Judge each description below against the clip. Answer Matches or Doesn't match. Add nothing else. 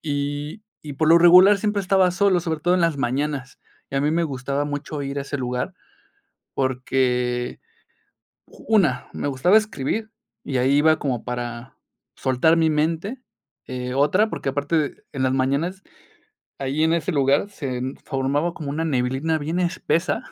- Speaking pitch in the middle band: Matches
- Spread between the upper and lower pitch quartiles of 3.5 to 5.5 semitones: Matches